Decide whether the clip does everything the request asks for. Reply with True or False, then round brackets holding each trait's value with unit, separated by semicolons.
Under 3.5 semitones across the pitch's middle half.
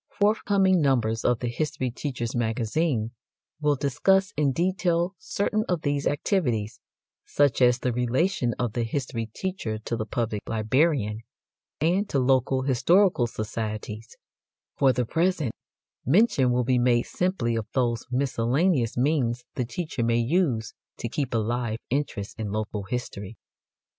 False (5.2 semitones)